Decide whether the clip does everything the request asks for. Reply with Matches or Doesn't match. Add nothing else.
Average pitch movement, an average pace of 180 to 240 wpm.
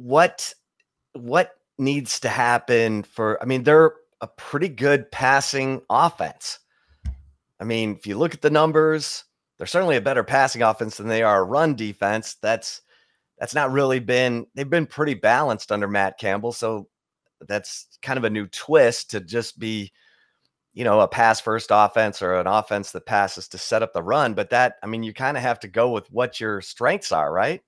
Matches